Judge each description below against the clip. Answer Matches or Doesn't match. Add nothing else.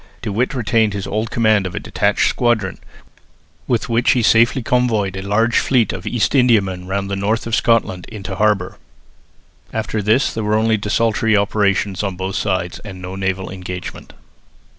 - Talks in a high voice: Doesn't match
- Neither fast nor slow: Matches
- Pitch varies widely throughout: Doesn't match